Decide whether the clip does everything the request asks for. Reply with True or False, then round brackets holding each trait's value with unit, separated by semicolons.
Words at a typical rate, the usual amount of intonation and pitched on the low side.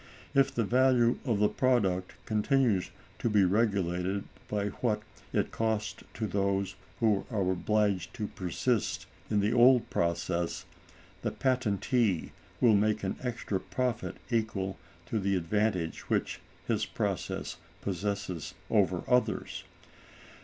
False (125 wpm; 3.5 semitones; 105 Hz)